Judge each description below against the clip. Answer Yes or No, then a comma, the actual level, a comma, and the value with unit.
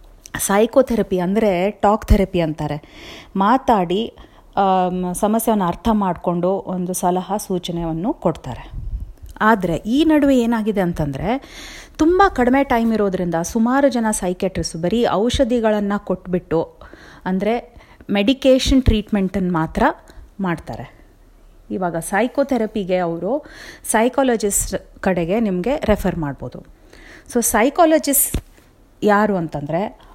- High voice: Yes, high, 200 Hz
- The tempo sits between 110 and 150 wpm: No, average, 90 wpm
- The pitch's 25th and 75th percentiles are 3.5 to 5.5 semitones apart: Yes, average, 4.9 semitones